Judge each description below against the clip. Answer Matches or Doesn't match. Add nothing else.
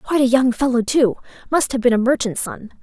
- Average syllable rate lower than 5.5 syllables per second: Doesn't match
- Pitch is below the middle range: Doesn't match